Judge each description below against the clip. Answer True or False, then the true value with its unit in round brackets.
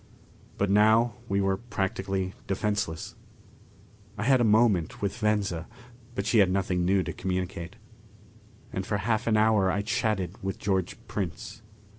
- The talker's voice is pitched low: True (100 Hz)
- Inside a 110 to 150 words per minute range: True (145 wpm)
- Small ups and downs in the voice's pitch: True (2.3 semitones)